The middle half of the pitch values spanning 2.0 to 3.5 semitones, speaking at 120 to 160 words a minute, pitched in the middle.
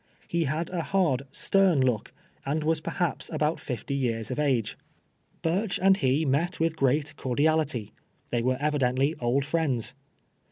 No: average, 4.0 semitones; average, 150 wpm; medium, 145 Hz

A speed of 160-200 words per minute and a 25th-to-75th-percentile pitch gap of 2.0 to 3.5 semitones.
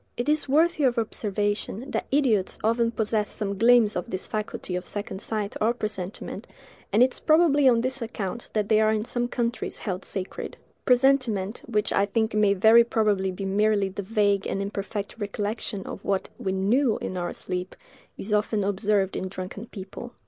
Yes: average, 180 wpm; average, 3.0 semitones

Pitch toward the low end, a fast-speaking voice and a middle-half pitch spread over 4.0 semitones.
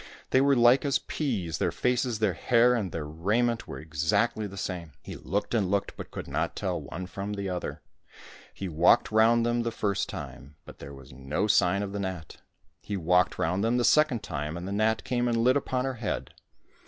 Yes: low, 100 Hz; fast, 215 wpm; average, 5.2 semitones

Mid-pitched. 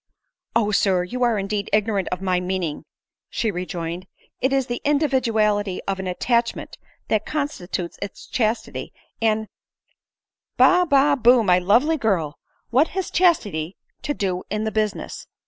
No: high, 215 Hz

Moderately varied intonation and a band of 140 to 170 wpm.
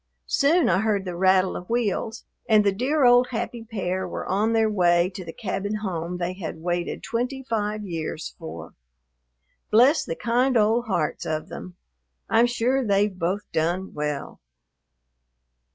Yes: average, 4.6 semitones; average, 155 wpm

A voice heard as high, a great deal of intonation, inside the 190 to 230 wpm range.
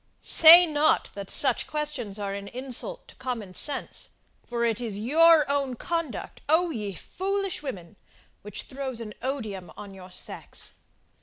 No: very high, 255 Hz; wide, 6.7 semitones; average, 150 wpm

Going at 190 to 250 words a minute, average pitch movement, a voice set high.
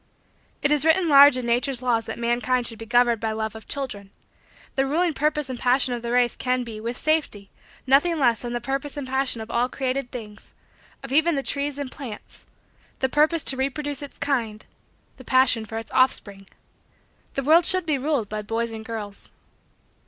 Yes: average, 195 wpm; average, 3.6 semitones; very high, 255 Hz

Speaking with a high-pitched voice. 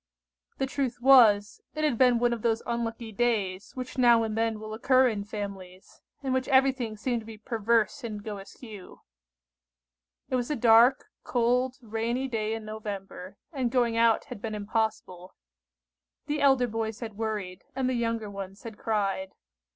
Yes: high, 225 Hz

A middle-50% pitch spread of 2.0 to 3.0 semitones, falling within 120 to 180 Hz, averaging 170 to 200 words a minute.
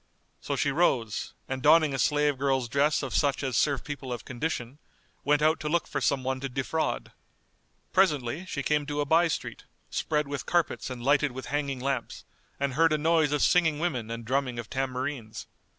Yes: narrow, 2.6 semitones; medium, 140 Hz; average, 195 wpm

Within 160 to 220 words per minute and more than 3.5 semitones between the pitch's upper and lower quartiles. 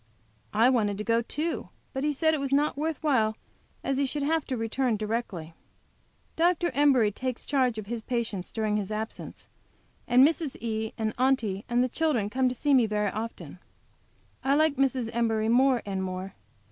Yes: average, 185 wpm; average, 4.2 semitones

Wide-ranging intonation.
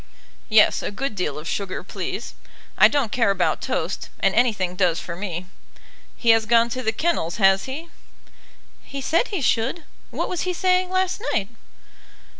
Yes: wide, 8.1 semitones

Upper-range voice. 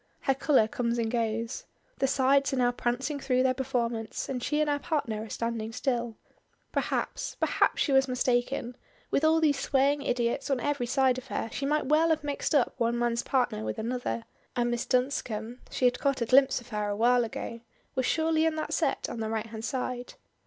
Yes: very high, 250 Hz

